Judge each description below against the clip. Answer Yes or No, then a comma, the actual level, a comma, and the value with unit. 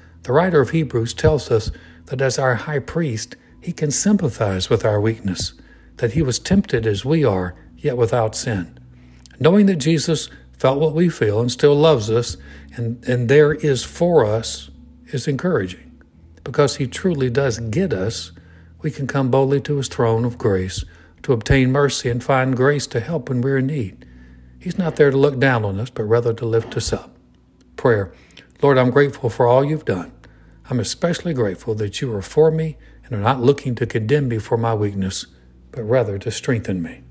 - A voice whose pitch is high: No, low, 120 Hz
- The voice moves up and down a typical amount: No, wide, 6.2 semitones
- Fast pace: No, average, 190 wpm